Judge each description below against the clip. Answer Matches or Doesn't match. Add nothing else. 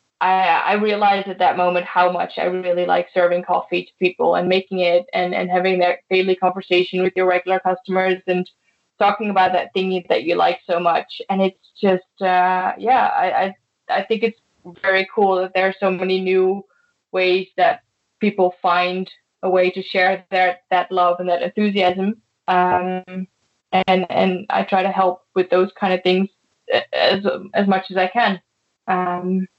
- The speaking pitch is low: Doesn't match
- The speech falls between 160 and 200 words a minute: Matches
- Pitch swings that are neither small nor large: Doesn't match